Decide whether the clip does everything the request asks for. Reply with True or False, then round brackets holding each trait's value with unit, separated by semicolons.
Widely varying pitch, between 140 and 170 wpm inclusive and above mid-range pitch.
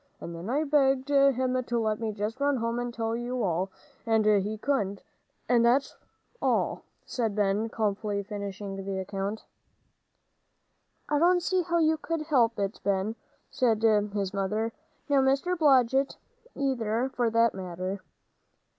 False (4.8 semitones; 145 wpm; 230 Hz)